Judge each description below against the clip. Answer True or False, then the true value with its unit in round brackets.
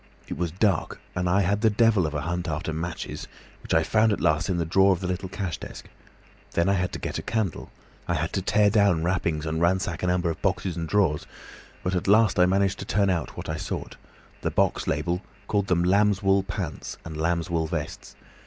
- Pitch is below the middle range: True (90 Hz)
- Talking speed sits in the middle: False (220 wpm)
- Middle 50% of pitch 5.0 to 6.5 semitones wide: False (2.9 semitones)